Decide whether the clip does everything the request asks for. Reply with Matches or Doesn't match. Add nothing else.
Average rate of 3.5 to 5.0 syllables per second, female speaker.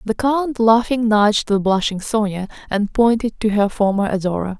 Matches